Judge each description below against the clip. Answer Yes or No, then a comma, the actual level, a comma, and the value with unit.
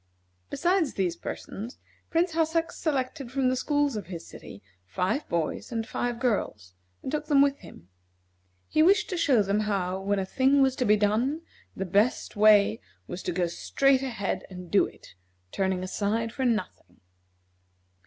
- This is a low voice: No, high, 225 Hz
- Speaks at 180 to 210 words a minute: No, average, 165 wpm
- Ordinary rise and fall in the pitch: No, wide, 6.4 semitones